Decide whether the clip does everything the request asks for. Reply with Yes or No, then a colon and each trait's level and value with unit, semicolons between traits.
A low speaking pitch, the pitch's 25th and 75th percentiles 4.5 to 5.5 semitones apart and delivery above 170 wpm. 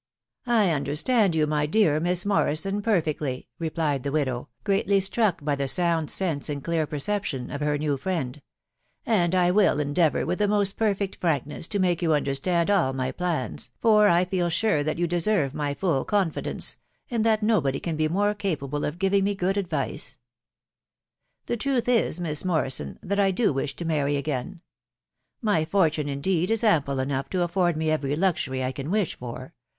No: medium, 165 Hz; average, 5.2 semitones; average, 185 wpm